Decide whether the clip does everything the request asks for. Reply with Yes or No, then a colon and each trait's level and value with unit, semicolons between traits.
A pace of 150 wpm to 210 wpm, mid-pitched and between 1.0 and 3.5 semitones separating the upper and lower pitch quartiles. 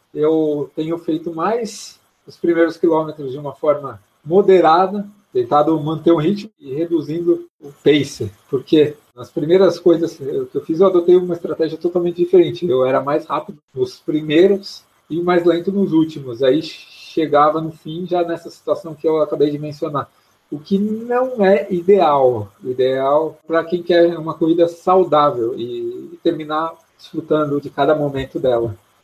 Yes: average, 155 wpm; medium, 165 Hz; average, 3.2 semitones